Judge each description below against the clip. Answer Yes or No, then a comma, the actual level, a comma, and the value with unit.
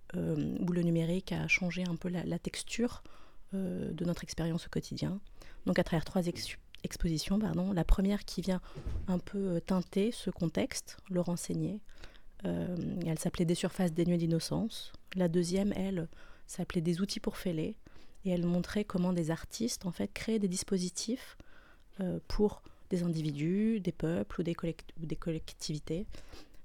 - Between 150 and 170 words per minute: Yes, average, 160 wpm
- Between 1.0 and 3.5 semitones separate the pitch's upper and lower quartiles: Yes, narrow, 2.4 semitones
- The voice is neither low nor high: Yes, medium, 180 Hz